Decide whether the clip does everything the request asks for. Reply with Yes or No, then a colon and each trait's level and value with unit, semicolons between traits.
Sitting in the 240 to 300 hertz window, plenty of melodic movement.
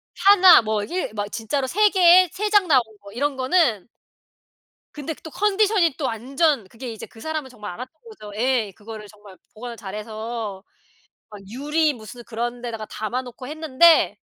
Yes: very high, 250 Hz; wide, 6.6 semitones